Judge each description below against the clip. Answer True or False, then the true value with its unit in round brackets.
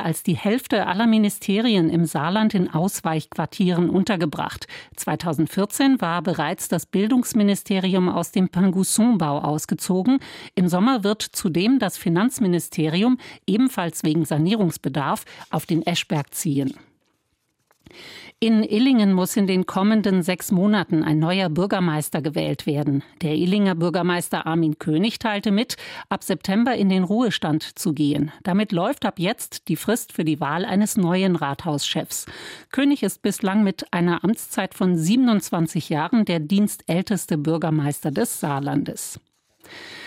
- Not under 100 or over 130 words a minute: True (125 wpm)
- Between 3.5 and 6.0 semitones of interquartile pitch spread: True (4.3 semitones)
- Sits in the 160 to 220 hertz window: True (185 Hz)